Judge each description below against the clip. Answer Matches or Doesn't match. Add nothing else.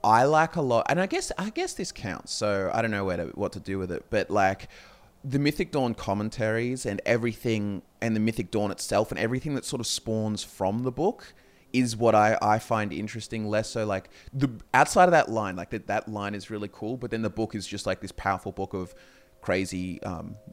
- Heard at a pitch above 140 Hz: Doesn't match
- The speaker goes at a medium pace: Doesn't match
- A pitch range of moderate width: Matches